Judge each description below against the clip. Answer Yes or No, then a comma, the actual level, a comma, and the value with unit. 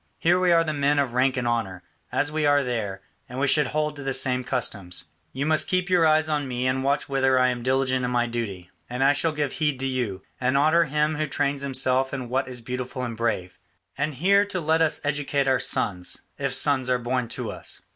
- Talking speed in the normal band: No, fast, 235 wpm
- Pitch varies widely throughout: No, average, 3.2 semitones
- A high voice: No, low, 135 Hz